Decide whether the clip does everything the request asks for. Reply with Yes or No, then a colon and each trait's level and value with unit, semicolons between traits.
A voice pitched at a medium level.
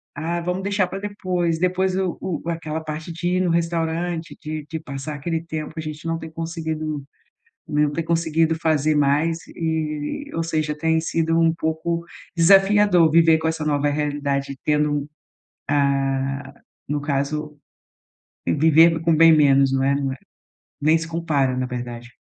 Yes: medium, 160 Hz